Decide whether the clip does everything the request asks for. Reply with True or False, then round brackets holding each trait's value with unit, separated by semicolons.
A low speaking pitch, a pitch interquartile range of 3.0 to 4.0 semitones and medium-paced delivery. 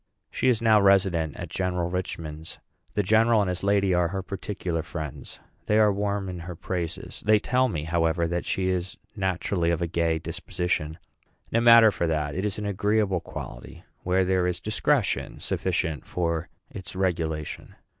True (90 Hz; 3.4 semitones; 170 wpm)